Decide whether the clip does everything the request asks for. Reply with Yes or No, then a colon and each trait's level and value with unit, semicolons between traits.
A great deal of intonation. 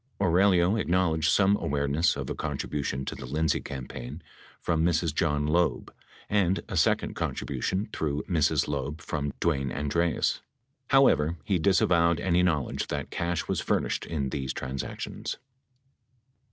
No: average, 3.5 semitones